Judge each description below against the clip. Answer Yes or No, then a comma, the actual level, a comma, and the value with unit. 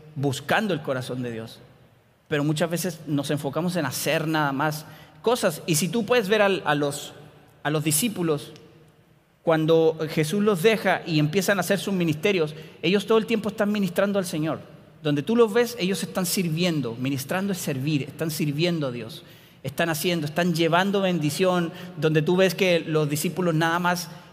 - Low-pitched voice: No, medium, 165 Hz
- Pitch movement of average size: Yes, average, 3.5 semitones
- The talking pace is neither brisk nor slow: Yes, average, 175 wpm